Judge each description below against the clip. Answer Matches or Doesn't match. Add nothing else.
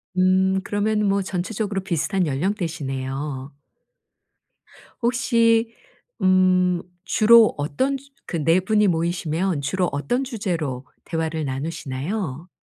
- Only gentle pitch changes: Doesn't match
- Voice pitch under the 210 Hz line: Matches